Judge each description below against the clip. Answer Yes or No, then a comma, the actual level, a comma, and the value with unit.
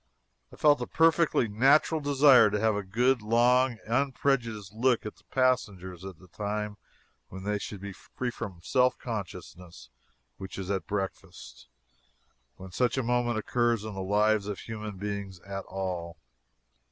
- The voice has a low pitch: Yes, low, 105 Hz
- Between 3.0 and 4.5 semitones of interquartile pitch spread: Yes, average, 4.2 semitones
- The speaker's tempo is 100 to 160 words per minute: Yes, average, 155 wpm